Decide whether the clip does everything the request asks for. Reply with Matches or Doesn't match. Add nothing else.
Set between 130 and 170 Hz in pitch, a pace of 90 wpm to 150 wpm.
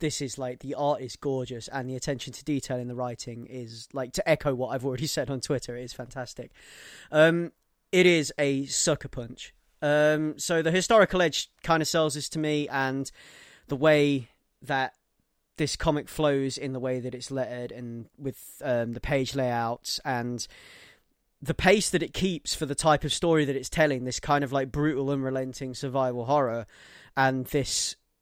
Doesn't match